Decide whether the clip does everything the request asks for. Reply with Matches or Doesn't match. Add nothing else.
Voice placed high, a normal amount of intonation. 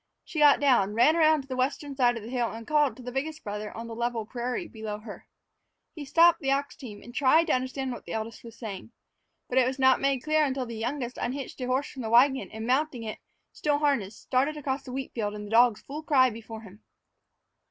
Matches